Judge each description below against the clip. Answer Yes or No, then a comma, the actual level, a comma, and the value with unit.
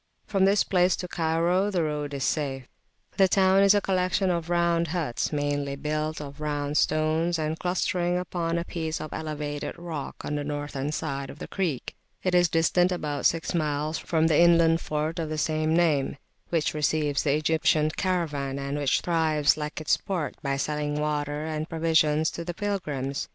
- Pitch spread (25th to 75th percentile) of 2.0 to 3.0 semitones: Yes, narrow, 2.6 semitones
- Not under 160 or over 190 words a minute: Yes, average, 180 wpm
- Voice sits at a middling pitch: Yes, medium, 155 Hz